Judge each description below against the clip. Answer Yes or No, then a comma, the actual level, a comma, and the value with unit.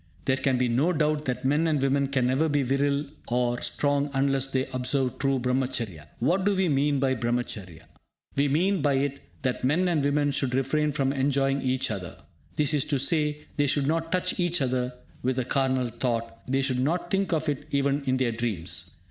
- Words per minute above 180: Yes, average, 200 wpm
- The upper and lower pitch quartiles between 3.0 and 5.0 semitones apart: No, narrow, 2.6 semitones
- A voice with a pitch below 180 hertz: Yes, low, 135 Hz